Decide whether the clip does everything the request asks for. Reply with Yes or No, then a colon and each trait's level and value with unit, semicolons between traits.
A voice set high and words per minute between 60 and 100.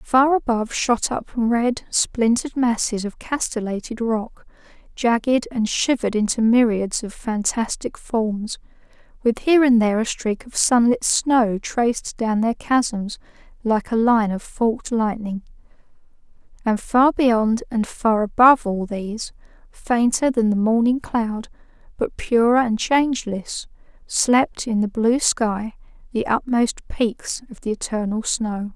No: high, 230 Hz; average, 140 wpm